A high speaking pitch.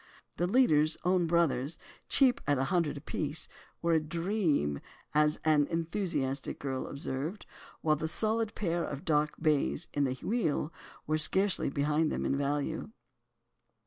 No: medium, 155 Hz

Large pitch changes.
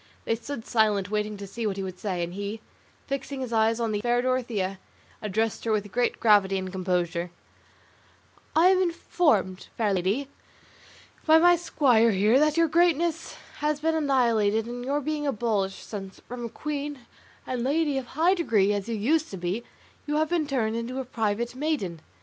Yes: wide, 6.2 semitones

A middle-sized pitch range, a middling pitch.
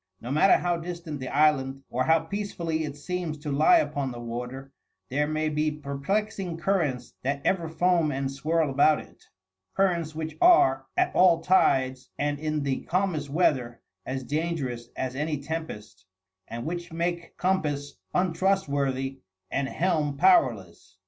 Yes: average, 4.0 semitones; medium, 150 Hz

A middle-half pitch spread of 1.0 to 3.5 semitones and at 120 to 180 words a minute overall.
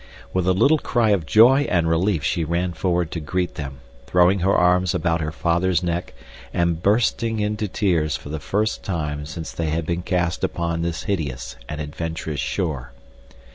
Yes: average, 2.9 semitones; average, 175 wpm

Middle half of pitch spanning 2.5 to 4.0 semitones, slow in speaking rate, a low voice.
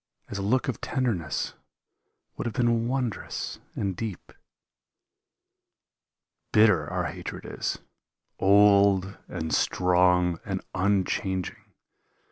Yes: average, 3.6 semitones; slow, 95 wpm; low, 100 Hz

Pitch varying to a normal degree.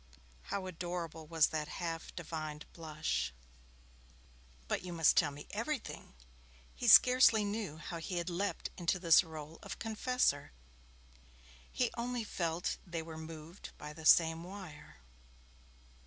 Yes: average, 3.8 semitones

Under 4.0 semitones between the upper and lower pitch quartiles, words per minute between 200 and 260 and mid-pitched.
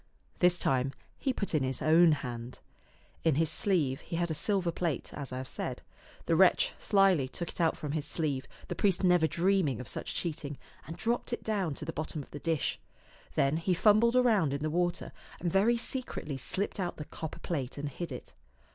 No: average, 4.7 semitones; fast, 205 wpm; medium, 165 Hz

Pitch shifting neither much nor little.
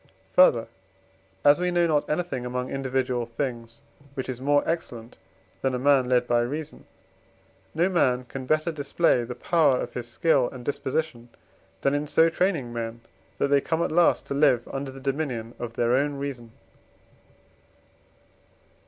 Yes: average, 3.8 semitones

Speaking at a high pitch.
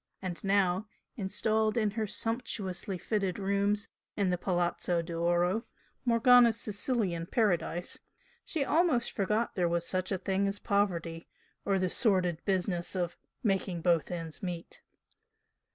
Yes: high, 195 Hz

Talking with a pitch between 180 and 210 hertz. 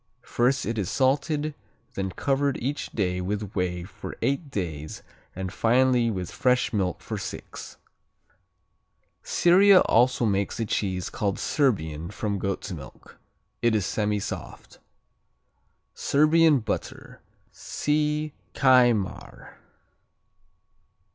No: low, 115 Hz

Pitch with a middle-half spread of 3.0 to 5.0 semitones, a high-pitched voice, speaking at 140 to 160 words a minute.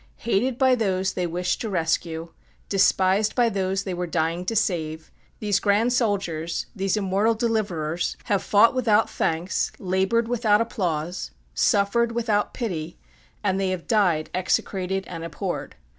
Yes: average, 3.8 semitones; high, 195 Hz; average, 145 wpm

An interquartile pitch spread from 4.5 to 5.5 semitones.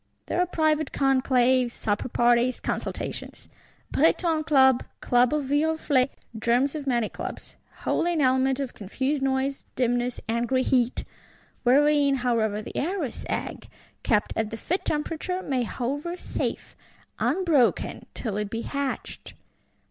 No: average, 3.5 semitones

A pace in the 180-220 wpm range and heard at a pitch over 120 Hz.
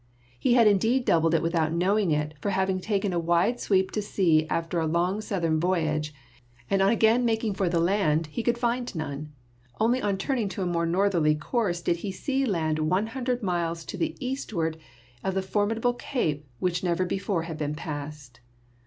Yes: average, 190 wpm; medium, 185 Hz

